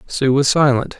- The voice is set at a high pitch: No, low, 135 Hz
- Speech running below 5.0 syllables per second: Yes, 4.7 syllables/s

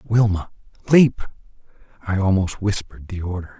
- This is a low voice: Yes, low, 100 Hz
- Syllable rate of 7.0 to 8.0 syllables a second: No, 5.1 syllables/s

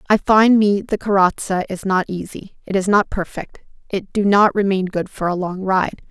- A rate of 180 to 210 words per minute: Yes, fast, 205 wpm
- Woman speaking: Yes, female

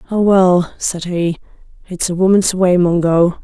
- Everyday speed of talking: Yes, average, 155 wpm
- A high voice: No, medium, 180 Hz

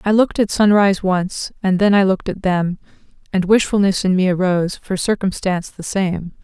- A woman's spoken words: Yes, female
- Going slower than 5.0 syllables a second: No, 5.5 syllables/s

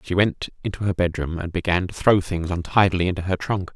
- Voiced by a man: Yes, male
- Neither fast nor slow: No, fast, 225 wpm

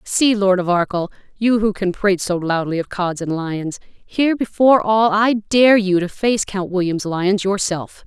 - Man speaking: No, female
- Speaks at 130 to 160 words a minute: No, average, 195 wpm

